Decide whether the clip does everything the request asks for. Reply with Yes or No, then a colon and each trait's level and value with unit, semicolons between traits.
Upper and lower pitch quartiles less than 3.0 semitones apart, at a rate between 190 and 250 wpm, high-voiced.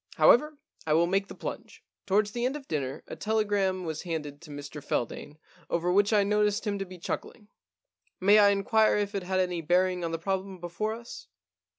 No: average, 3.6 semitones; average, 200 wpm; high, 195 Hz